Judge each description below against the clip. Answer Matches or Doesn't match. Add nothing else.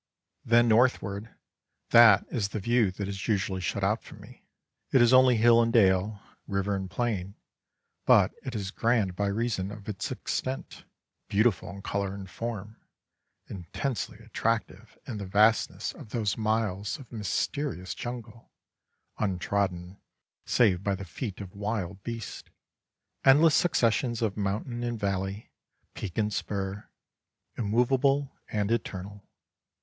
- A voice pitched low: Matches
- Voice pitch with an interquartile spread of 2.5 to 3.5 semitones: Matches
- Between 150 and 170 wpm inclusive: Doesn't match